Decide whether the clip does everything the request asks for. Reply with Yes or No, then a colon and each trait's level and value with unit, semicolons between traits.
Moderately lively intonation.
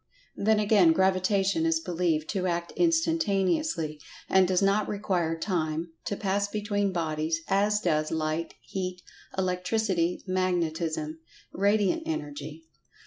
Yes: average, 3.7 semitones